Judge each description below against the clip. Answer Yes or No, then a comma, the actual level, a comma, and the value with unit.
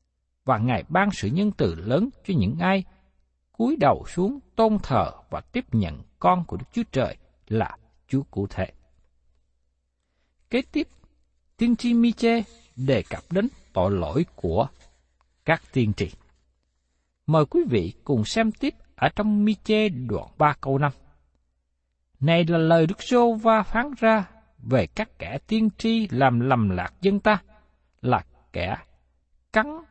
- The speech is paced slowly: Yes, slow, 150 wpm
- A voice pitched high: No, low, 135 Hz